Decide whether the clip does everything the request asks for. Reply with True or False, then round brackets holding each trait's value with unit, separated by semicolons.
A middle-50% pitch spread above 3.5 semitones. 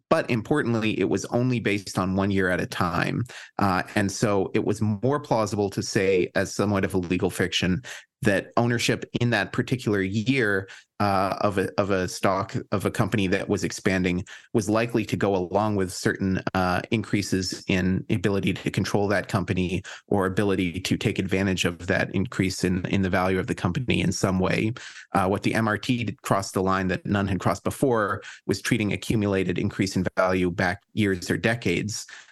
False (2.9 semitones)